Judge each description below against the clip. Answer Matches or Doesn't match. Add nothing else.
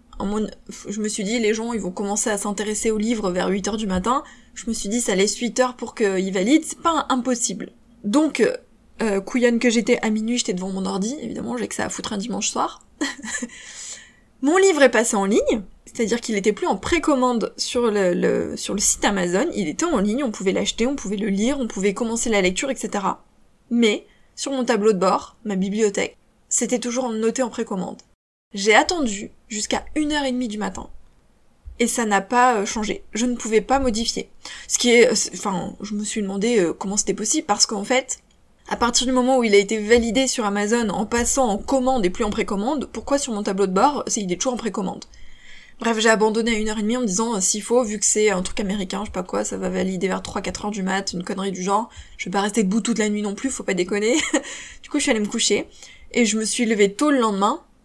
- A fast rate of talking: Matches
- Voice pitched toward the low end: Doesn't match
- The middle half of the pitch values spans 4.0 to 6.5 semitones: Doesn't match